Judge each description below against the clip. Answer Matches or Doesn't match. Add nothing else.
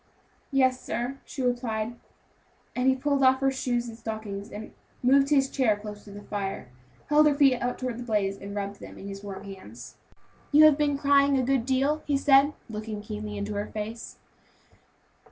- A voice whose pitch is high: Matches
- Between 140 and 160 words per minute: Doesn't match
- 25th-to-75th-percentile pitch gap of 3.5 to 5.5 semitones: Matches